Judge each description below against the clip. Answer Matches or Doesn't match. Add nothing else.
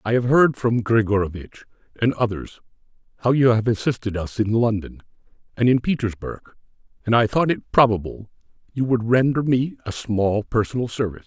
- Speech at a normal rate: Matches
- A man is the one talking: Matches